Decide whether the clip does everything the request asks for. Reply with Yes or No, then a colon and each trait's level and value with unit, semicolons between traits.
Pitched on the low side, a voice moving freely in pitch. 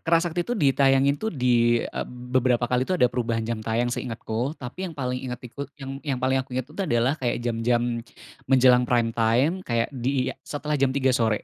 No: low, 125 Hz; average, 2.7 semitones